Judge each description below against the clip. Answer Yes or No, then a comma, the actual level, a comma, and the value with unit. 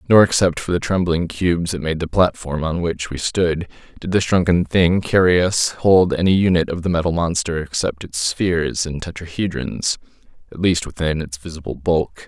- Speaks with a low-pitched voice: Yes, very low, 85 Hz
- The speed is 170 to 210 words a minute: Yes, average, 180 wpm